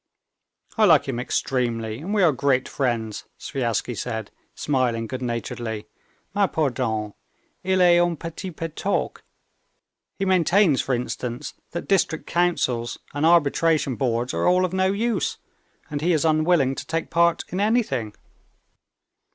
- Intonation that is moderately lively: No, wide, 6.4 semitones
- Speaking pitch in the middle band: Yes, medium, 150 Hz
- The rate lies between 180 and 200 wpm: No, average, 145 wpm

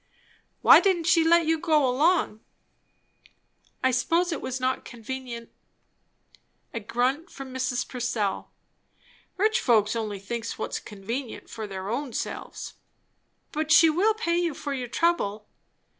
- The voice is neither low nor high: No, very high, 260 Hz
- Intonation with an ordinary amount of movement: No, wide, 6.2 semitones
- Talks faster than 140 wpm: No, slow, 135 wpm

